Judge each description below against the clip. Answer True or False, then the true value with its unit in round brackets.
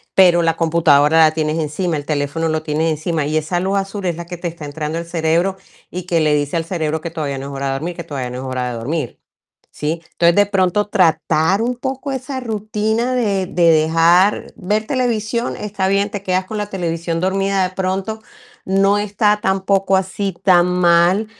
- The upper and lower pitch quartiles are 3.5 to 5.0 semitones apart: True (3.9 semitones)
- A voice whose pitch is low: False (175 Hz)